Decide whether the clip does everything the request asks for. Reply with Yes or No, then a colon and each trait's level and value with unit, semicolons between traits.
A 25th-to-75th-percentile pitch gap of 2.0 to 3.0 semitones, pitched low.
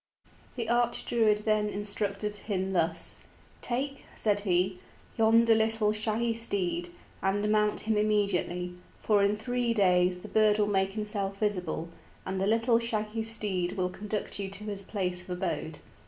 No: narrow, 2.4 semitones; high, 210 Hz